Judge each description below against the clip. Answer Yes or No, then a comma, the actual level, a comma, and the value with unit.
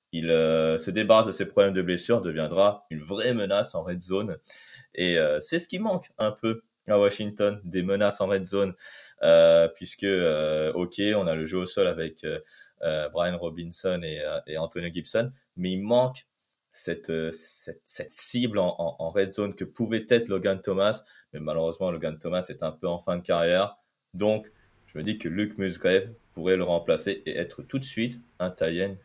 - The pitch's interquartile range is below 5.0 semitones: Yes, average, 4.1 semitones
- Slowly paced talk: No, average, 200 wpm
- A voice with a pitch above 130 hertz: No, very low, 95 Hz